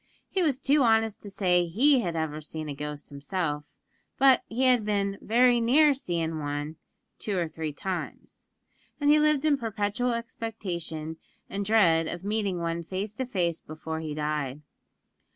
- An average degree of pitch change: No, wide, 6.6 semitones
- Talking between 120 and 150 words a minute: No, average, 165 wpm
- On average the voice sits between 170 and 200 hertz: Yes, high, 190 Hz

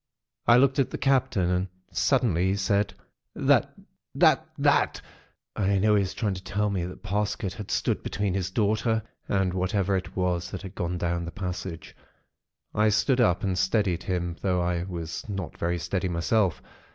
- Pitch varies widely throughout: No, average, 2.7 semitones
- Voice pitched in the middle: No, very low, 95 Hz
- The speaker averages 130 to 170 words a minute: No, average, 185 wpm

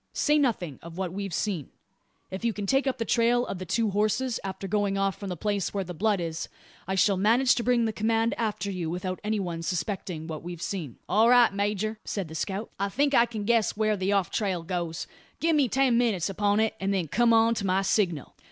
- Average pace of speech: No, fast, 235 wpm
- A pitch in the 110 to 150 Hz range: No, high, 200 Hz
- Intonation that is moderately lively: Yes, average, 3.7 semitones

